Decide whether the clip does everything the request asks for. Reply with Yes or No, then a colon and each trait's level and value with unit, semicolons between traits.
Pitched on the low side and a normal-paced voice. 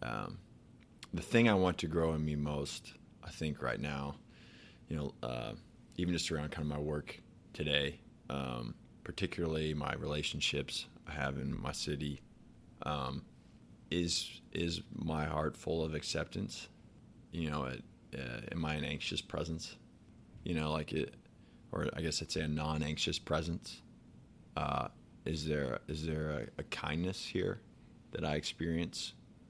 Yes: very low, 75 Hz; average, 155 wpm